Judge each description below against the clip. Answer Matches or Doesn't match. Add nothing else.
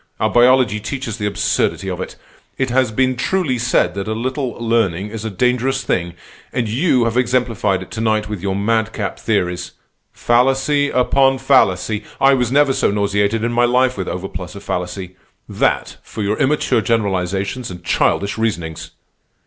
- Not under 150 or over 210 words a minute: Matches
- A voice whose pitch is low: Matches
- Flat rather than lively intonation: Doesn't match